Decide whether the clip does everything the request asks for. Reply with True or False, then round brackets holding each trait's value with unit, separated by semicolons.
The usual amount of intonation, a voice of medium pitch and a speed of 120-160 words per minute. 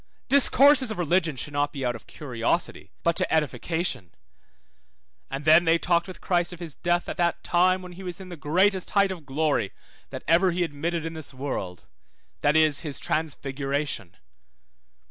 False (3.7 semitones; 165 Hz; 175 wpm)